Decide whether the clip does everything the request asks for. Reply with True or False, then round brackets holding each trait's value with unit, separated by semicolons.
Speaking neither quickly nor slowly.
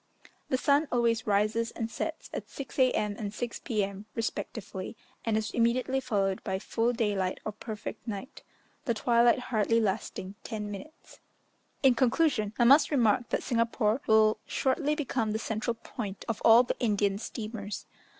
True (155 wpm)